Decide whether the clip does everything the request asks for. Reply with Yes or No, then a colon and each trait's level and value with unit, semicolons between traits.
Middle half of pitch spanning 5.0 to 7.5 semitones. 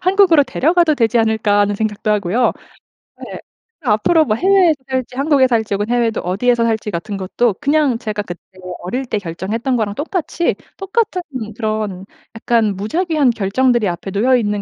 Yes: average, 5.3 semitones